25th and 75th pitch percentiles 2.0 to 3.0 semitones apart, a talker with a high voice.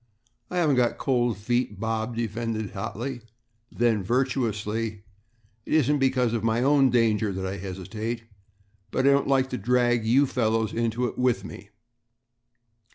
No: narrow, 2.6 semitones; low, 115 Hz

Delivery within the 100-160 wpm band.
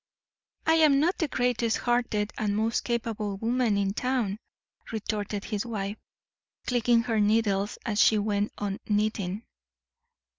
Yes: slow, 135 wpm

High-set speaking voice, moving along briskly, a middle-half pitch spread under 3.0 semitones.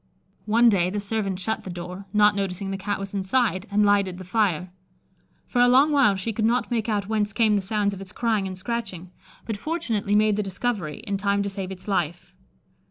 Yes: high, 205 Hz; fast, 215 wpm; narrow, 2.5 semitones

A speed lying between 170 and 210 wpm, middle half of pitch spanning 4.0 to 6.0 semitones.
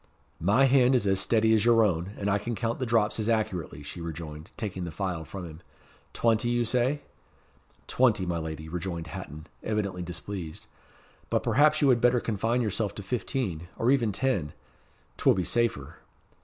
Yes: average, 180 wpm; wide, 5.4 semitones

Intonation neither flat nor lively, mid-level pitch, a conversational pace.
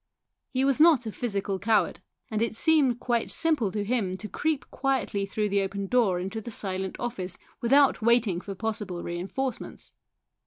No: average, 4.3 semitones; high, 220 Hz; average, 165 wpm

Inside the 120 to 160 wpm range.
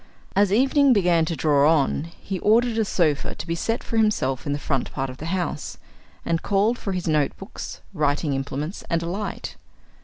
No: average, 190 wpm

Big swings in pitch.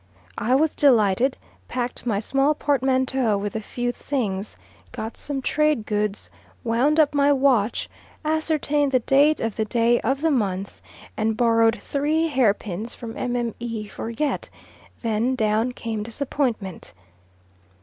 No: average, 4.3 semitones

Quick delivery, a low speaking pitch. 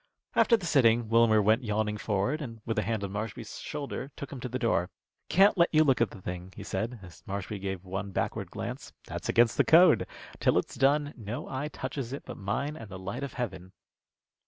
Yes: fast, 215 wpm; low, 115 Hz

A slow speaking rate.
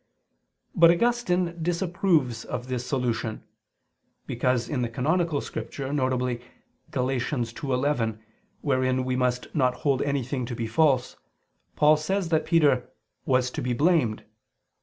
Yes: slow, 125 wpm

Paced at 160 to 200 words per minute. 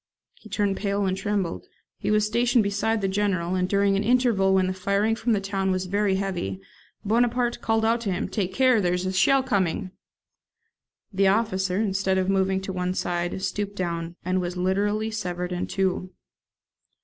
Yes: average, 185 wpm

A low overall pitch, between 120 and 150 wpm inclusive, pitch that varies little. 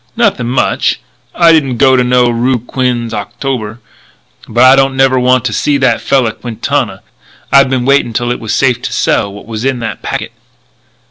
No: low, 125 Hz; average, 180 wpm; narrow, 2.2 semitones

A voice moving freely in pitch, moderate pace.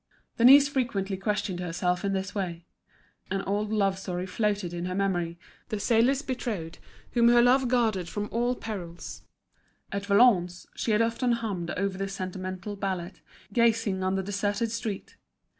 No: average, 3.6 semitones; average, 155 wpm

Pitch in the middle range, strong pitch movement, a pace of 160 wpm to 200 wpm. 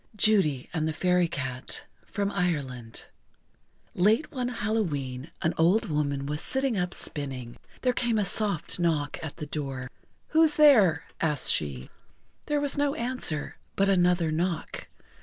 No: medium, 175 Hz; wide, 6.9 semitones; average, 140 wpm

